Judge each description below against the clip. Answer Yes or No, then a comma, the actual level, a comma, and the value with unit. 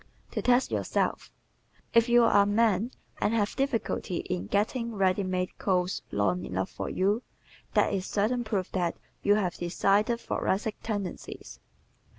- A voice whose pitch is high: Yes, high, 205 Hz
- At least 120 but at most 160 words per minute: Yes, average, 155 wpm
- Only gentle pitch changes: No, average, 3.8 semitones